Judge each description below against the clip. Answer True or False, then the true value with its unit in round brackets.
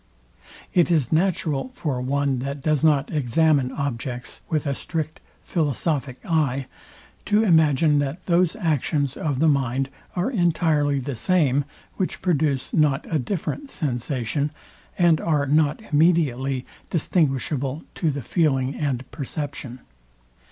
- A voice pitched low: False (145 Hz)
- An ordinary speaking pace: False (125 wpm)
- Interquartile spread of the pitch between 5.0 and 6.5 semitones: False (3.2 semitones)